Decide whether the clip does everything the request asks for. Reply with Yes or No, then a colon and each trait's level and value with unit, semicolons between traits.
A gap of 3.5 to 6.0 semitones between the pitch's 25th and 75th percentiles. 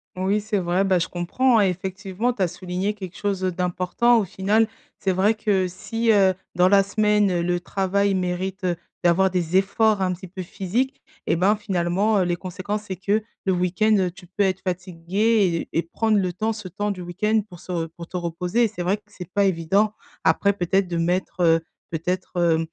No: narrow, 2.6 semitones